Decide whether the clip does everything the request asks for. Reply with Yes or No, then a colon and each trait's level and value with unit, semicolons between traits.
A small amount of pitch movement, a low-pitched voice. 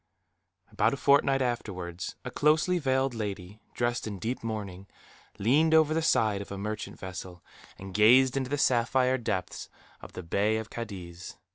No: average, 5.2 semitones; low, 110 Hz